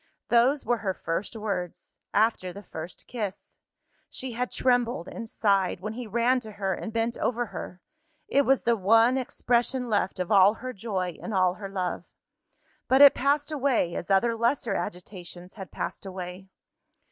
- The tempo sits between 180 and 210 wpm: No, average, 170 wpm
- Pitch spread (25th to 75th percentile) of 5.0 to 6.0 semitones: No, average, 4.4 semitones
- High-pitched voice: Yes, high, 220 Hz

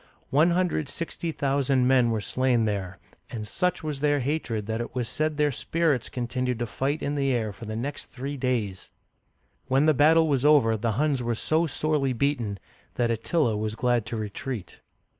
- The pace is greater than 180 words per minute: Yes, average, 190 wpm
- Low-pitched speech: Yes, low, 130 Hz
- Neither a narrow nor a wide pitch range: Yes, average, 4.4 semitones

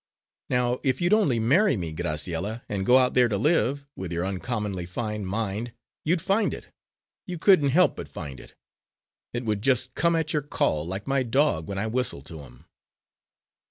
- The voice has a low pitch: Yes, low, 115 Hz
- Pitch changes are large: Yes, wide, 7.0 semitones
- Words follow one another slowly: No, average, 185 wpm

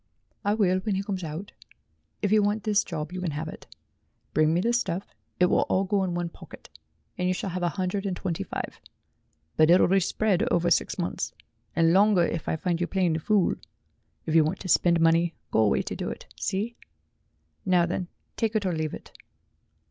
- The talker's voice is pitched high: No, medium, 180 Hz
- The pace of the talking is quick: Yes, fast, 210 wpm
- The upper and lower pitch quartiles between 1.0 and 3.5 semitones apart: Yes, average, 3.0 semitones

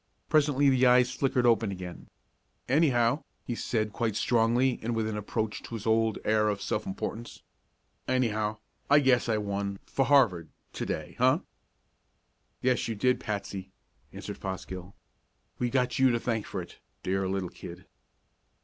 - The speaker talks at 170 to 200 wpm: No, average, 155 wpm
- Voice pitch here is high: No, low, 115 Hz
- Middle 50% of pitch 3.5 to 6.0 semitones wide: Yes, average, 3.8 semitones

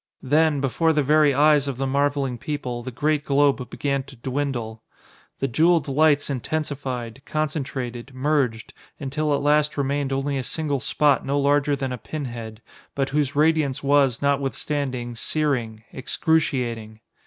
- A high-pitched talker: No, medium, 140 Hz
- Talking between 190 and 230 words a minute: No, average, 145 wpm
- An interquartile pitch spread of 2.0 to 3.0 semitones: Yes, narrow, 2.5 semitones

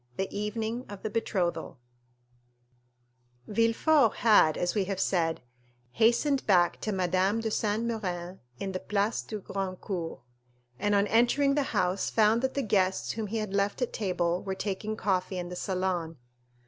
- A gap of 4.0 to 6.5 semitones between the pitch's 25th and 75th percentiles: No, average, 3.3 semitones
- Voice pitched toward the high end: Yes, high, 200 Hz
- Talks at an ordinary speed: Yes, average, 160 wpm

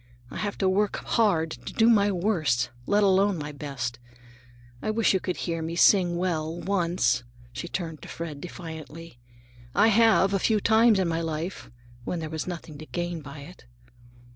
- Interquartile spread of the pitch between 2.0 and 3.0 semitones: No, average, 4.0 semitones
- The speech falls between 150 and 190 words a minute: Yes, average, 180 wpm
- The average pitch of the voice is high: No, medium, 175 Hz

